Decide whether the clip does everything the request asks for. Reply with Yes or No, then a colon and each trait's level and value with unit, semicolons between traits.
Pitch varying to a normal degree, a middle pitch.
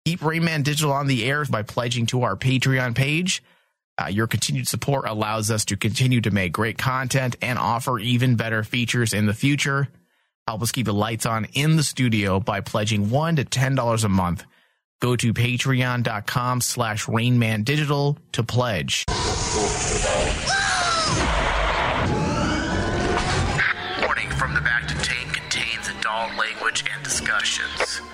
No: average, 3.4 semitones; low, 125 Hz